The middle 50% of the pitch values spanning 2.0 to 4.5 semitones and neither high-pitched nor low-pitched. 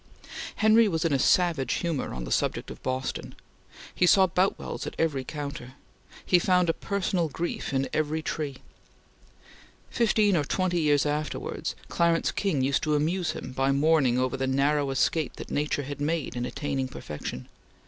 Yes: average, 4.2 semitones; medium, 150 Hz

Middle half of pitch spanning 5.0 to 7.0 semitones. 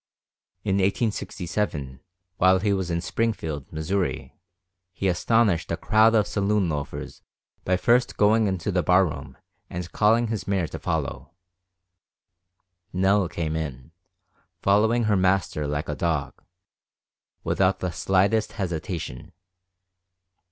No: average, 4.0 semitones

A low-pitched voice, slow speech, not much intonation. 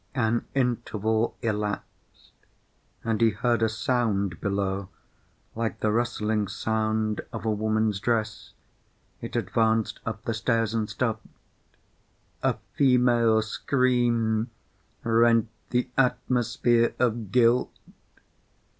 Yes: low, 115 Hz; slow, 100 wpm; narrow, 1.7 semitones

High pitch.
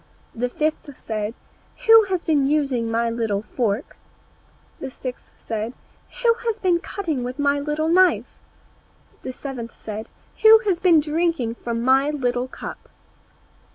Yes: very high, 275 Hz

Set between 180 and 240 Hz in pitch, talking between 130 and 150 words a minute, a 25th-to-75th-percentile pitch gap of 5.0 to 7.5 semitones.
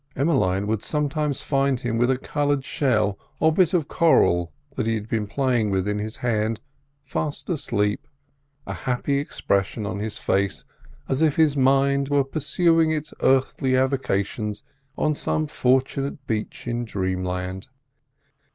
No: low, 130 Hz; average, 145 wpm; average, 5.3 semitones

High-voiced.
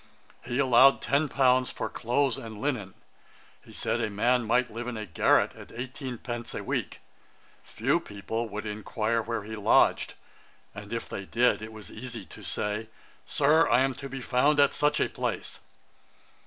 No: low, 120 Hz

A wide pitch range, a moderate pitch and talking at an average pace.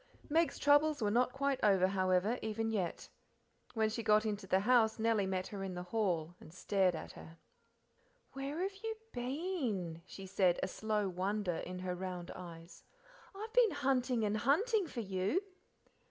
No: wide, 6.1 semitones; high, 215 Hz; average, 170 wpm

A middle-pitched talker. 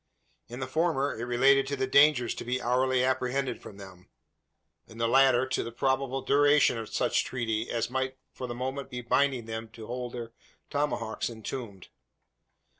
No: low, 125 Hz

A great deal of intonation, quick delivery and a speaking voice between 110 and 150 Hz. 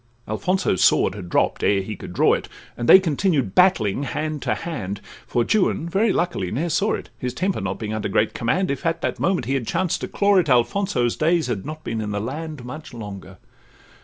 Yes: wide, 8.0 semitones; fast, 215 wpm; low, 135 Hz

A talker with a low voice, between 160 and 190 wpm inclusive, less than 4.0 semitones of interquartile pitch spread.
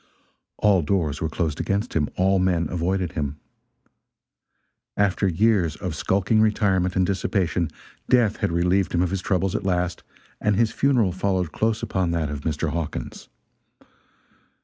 No: very low, 90 Hz; average, 150 wpm; average, 3.0 semitones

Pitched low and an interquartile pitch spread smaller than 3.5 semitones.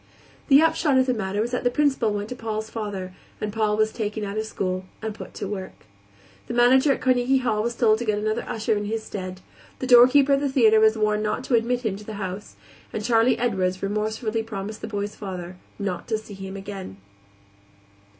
No: high, 215 Hz; average, 2.9 semitones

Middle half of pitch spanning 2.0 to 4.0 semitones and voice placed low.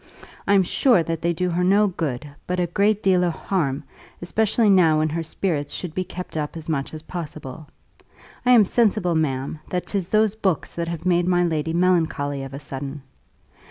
No: average, 3.3 semitones; medium, 170 Hz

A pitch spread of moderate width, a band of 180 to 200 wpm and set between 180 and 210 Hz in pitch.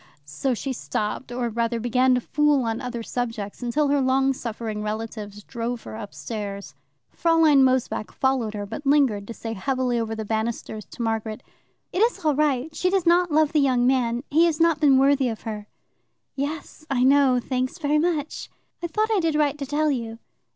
No: average, 4.6 semitones; average, 190 wpm; very high, 255 Hz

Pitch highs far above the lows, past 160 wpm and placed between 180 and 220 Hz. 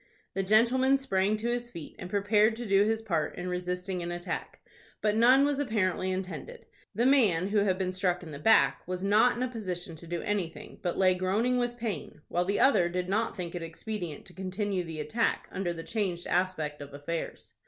No: average, 4.0 semitones; fast, 205 wpm; high, 190 Hz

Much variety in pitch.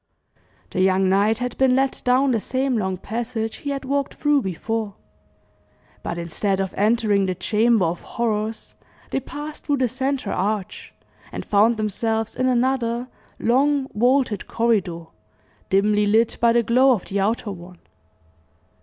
No: average, 4.2 semitones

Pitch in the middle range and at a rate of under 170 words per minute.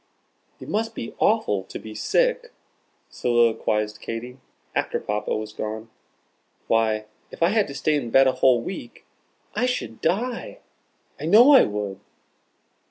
No: low, 125 Hz; average, 145 wpm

